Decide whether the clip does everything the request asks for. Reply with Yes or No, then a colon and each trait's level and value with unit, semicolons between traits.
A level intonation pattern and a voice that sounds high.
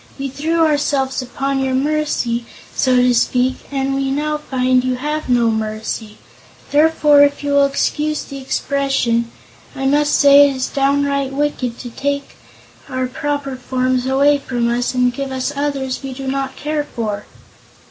Yes: narrow, 2.1 semitones; very high, 270 Hz